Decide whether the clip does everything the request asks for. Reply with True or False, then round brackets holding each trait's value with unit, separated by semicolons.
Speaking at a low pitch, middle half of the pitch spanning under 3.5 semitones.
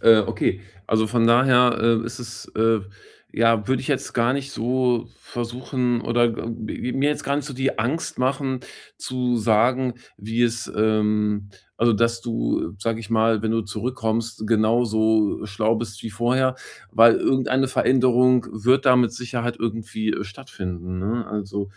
True (115 Hz; 2.4 semitones)